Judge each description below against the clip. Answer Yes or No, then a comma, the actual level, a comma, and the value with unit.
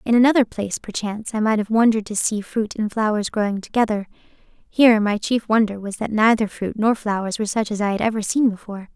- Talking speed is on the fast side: Yes, fast, 220 wpm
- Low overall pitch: No, high, 215 Hz